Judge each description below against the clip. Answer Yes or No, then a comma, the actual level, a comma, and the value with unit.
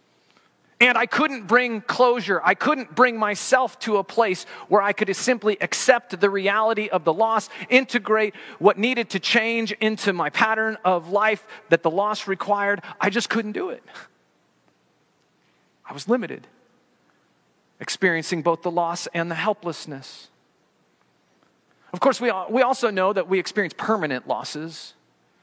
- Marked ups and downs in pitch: No, average, 4.4 semitones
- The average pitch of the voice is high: Yes, high, 205 Hz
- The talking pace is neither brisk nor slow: Yes, average, 145 wpm